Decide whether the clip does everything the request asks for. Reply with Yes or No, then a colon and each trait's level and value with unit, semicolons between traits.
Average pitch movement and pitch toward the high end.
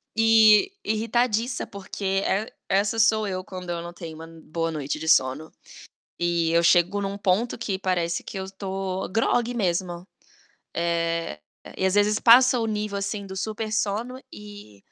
Yes: average, 4.0 semitones; high, 195 Hz